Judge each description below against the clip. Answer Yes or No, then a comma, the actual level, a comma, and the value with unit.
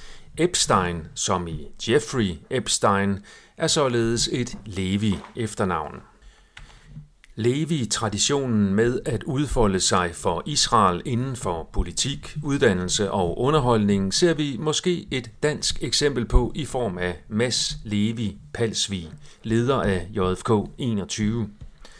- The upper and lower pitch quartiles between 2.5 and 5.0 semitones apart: No, wide, 5.6 semitones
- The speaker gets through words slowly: Yes, slow, 110 wpm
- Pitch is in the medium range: No, low, 115 Hz